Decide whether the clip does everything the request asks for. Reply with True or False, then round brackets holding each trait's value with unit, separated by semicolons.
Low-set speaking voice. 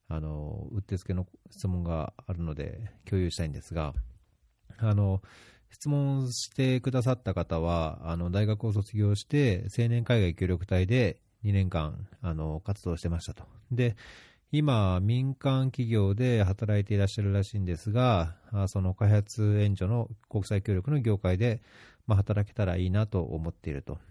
True (100 Hz)